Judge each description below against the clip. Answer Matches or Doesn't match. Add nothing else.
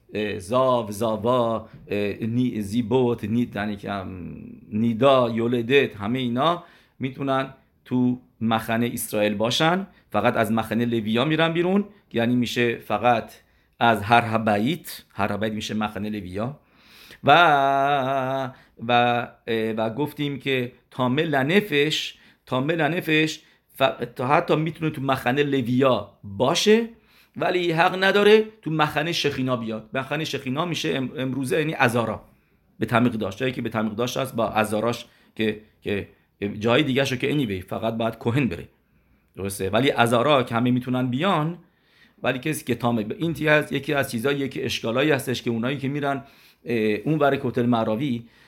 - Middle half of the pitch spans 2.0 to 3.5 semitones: Doesn't match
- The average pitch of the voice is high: Doesn't match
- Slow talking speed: Matches